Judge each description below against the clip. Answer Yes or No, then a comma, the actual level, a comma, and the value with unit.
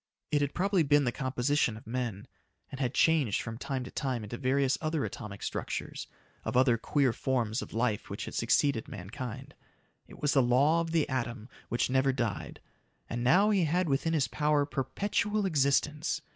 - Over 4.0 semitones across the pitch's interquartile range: No, average, 3.7 semitones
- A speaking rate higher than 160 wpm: Yes, average, 180 wpm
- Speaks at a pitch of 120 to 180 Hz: Yes, low, 135 Hz